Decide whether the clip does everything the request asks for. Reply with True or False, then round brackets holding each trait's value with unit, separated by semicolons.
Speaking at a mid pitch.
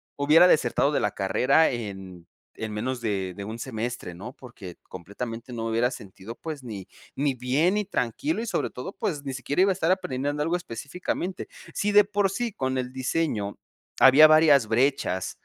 False (130 Hz)